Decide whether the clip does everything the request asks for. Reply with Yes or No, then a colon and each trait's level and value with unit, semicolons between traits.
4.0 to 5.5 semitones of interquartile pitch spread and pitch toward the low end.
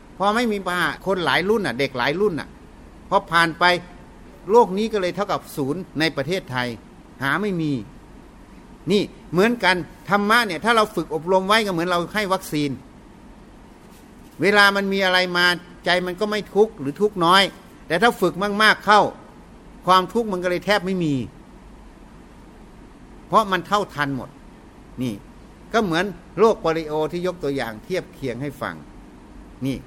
No: average, 4.4 semitones; medium, 180 Hz